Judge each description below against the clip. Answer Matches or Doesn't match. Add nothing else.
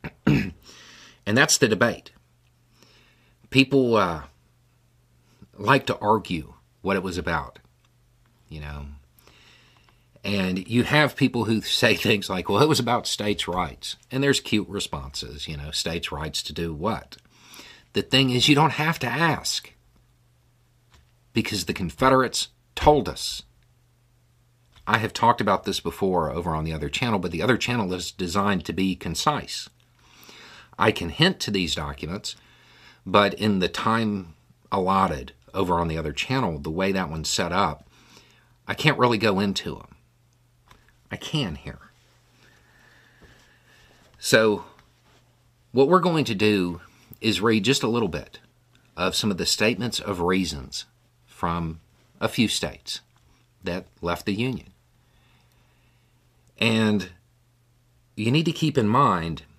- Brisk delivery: Doesn't match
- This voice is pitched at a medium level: Doesn't match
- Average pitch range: Doesn't match